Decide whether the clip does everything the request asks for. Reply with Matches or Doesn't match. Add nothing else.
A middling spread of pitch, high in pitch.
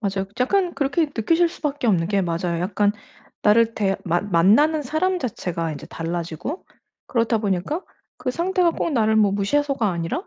Doesn't match